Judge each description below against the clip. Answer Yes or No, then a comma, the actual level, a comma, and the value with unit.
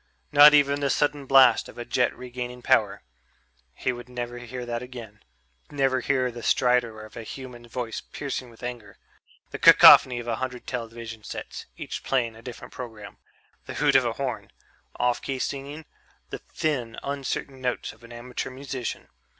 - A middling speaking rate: Yes, average, 170 wpm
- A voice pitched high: No, low, 125 Hz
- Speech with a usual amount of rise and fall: No, narrow, 2.0 semitones